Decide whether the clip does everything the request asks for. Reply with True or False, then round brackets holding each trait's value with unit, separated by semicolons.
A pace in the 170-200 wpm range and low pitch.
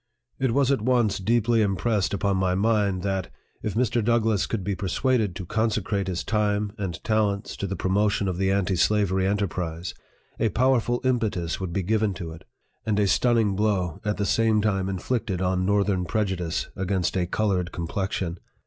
True (175 wpm; 100 Hz)